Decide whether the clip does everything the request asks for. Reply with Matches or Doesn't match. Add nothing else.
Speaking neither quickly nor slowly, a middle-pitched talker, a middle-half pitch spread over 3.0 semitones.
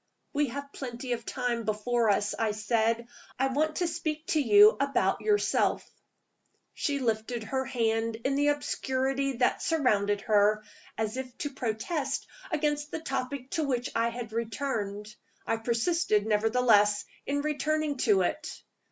Doesn't match